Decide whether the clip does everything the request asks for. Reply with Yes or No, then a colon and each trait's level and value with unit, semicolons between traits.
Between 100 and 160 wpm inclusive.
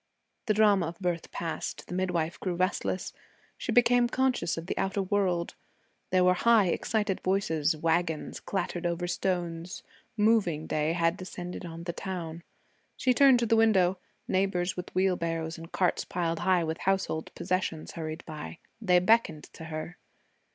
Yes: average, 155 wpm